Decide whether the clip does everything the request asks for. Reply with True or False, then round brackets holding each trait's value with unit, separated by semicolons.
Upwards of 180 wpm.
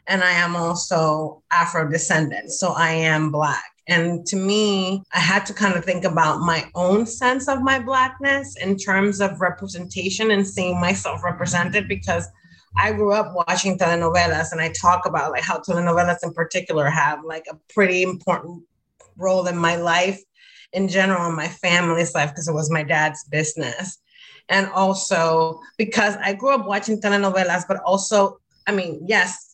False (170 wpm)